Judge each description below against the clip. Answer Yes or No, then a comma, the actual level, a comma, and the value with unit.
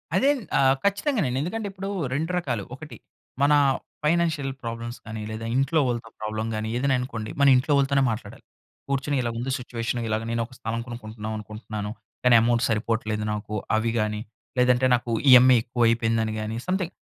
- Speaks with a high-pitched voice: No, low, 120 Hz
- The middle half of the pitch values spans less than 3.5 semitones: No, average, 3.9 semitones